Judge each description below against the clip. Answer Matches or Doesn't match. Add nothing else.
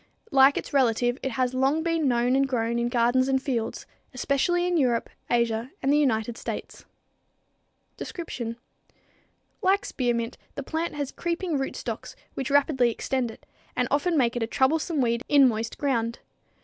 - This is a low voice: Doesn't match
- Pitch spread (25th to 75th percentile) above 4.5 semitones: Doesn't match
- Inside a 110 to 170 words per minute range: Matches